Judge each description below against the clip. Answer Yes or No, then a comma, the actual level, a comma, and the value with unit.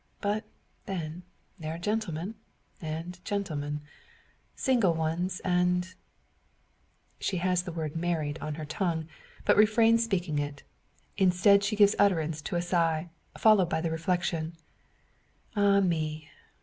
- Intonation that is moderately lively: Yes, average, 3.8 semitones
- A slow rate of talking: Yes, slow, 130 wpm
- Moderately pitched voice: Yes, medium, 175 Hz